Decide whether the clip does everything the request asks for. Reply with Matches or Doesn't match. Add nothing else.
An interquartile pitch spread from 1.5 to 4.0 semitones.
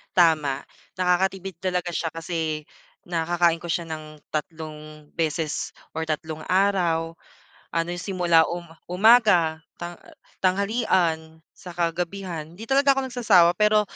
Matches